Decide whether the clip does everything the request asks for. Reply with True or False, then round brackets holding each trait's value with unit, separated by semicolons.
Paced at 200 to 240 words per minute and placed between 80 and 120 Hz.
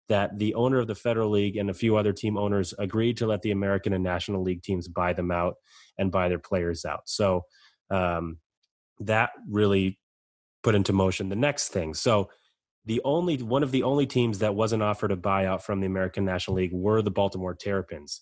True (205 wpm; 100 Hz)